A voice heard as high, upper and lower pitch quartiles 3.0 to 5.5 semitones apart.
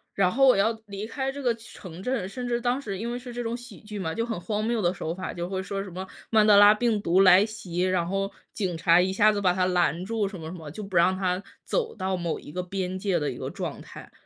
Yes: high, 195 Hz; average, 3.7 semitones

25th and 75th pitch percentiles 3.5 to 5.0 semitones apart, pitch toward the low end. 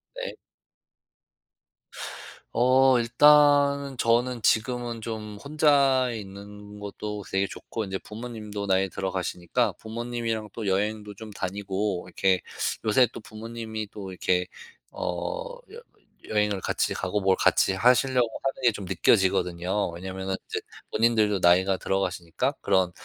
Yes: average, 3.9 semitones; low, 105 Hz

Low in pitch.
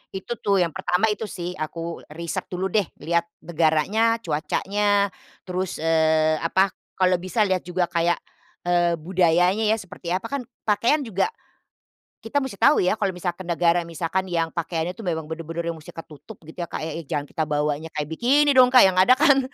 No: medium, 180 Hz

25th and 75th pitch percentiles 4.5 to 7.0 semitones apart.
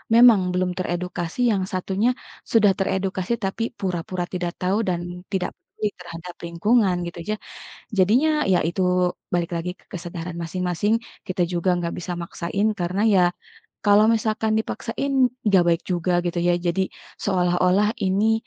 No: average, 2.9 semitones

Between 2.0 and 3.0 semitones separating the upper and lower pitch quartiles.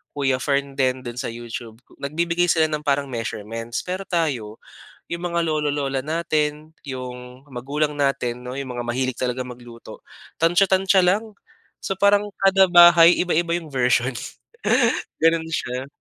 No: average, 5.3 semitones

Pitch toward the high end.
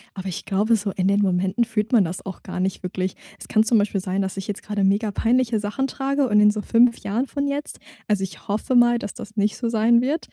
Yes: high, 210 Hz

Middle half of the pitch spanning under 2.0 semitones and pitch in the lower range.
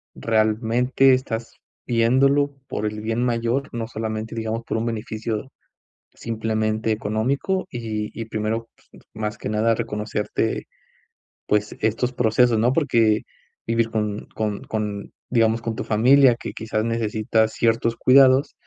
Yes: narrow, 1.6 semitones; low, 115 Hz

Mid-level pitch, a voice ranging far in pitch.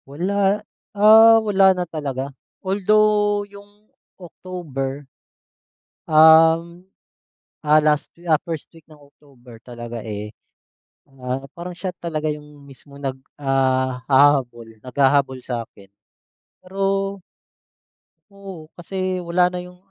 Yes: medium, 155 Hz; wide, 5.7 semitones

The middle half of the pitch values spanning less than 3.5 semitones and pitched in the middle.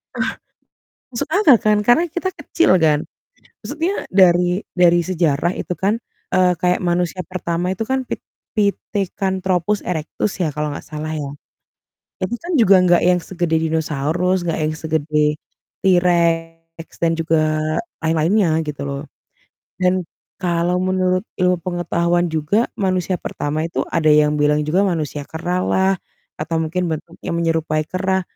Yes: average, 2.8 semitones; medium, 175 Hz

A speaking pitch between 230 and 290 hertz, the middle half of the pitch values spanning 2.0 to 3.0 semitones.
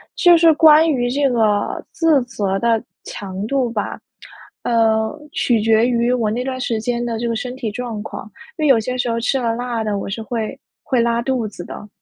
Yes: high, 235 Hz; narrow, 2.4 semitones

